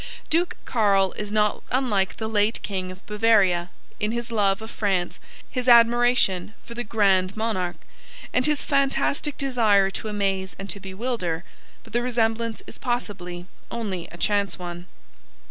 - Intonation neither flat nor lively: Yes, average, 3.7 semitones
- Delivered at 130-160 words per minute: Yes, average, 150 wpm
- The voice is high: Yes, high, 210 Hz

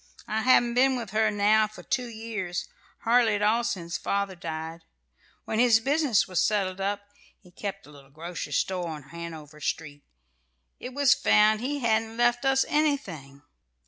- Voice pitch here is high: Yes, high, 210 Hz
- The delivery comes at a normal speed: Yes, average, 165 wpm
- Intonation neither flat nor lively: No, wide, 5.7 semitones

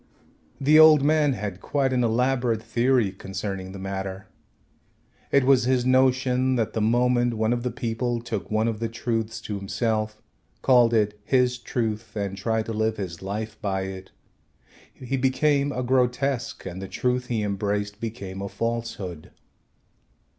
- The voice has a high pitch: No, low, 115 Hz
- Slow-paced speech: No, average, 155 wpm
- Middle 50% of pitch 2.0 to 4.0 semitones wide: Yes, average, 3.6 semitones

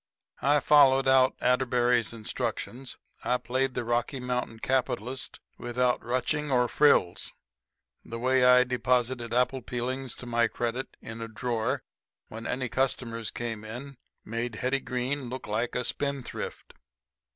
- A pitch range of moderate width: No, narrow, 1.8 semitones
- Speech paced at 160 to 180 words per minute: No, slow, 135 wpm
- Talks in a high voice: No, low, 125 Hz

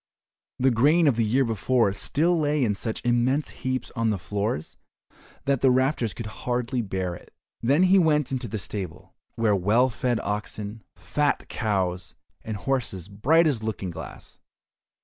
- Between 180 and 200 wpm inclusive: No, average, 165 wpm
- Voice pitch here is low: Yes, low, 120 Hz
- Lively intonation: No, average, 4.6 semitones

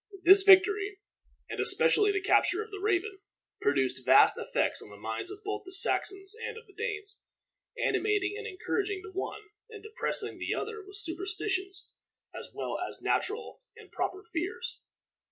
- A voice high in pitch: Yes, very high, 400 Hz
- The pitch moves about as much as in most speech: No, narrow, 1.9 semitones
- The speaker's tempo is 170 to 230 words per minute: No, average, 160 wpm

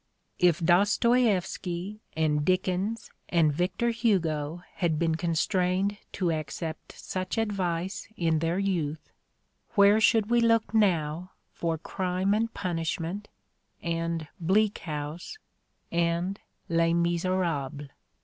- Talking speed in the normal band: No, slow, 105 wpm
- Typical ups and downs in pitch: Yes, average, 3.4 semitones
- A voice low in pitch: No, medium, 175 Hz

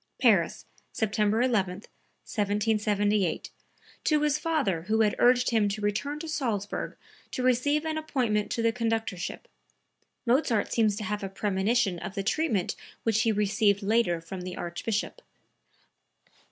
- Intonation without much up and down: No, average, 3.4 semitones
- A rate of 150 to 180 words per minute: No, average, 140 wpm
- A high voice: Yes, high, 215 Hz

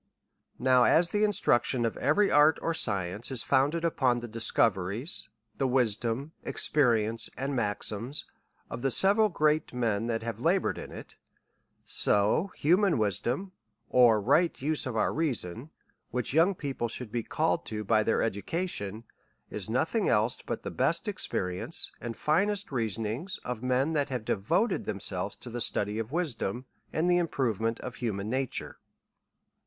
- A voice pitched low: Yes, low, 125 Hz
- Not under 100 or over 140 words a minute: No, average, 160 wpm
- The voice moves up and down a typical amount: No, wide, 5.8 semitones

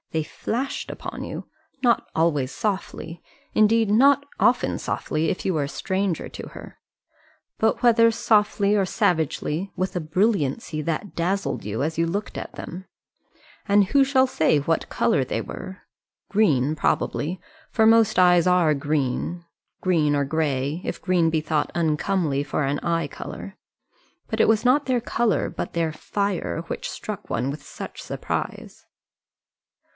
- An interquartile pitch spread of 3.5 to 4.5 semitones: No, wide, 5.4 semitones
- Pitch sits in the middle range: Yes, medium, 175 Hz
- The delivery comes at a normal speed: Yes, average, 155 wpm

